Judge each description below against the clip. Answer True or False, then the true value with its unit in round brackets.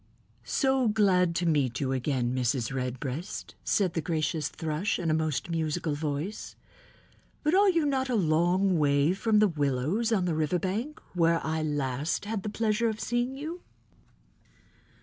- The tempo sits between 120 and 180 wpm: True (160 wpm)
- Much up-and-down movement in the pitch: True (6.5 semitones)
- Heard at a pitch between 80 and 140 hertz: False (170 Hz)